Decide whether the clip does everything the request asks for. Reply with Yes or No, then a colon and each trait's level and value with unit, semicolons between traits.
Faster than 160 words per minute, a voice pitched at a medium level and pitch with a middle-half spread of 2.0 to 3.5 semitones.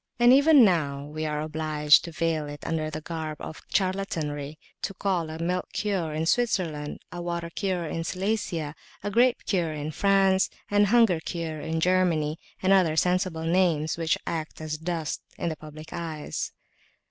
Yes: average, 170 wpm; medium, 165 Hz; average, 3.2 semitones